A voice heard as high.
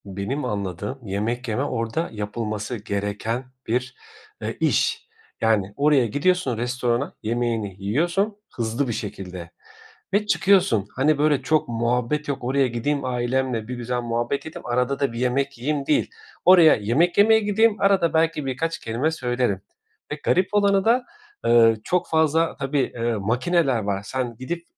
No: low, 125 Hz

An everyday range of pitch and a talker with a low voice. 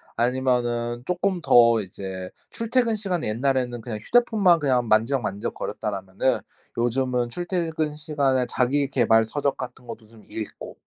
Yes: average, 4.9 semitones; low, 125 Hz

